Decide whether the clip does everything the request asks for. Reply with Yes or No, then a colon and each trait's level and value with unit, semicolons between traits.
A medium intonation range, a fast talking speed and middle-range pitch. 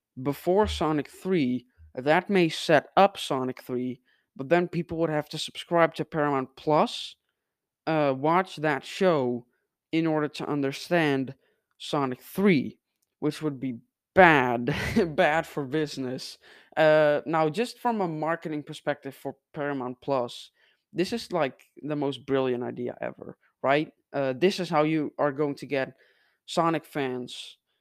No: average, 3.5 semitones; average, 140 wpm; medium, 150 Hz